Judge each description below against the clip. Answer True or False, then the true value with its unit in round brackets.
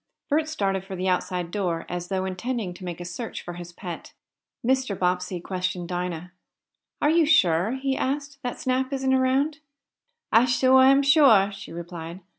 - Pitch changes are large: True (6.7 semitones)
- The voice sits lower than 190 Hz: False (195 Hz)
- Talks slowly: False (170 wpm)